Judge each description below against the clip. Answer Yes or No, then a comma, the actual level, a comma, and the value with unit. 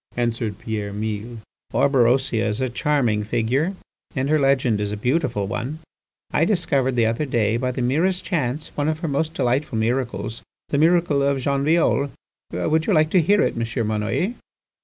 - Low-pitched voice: Yes, low, 130 Hz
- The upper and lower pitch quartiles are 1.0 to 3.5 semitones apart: No, average, 5.0 semitones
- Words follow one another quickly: No, average, 175 wpm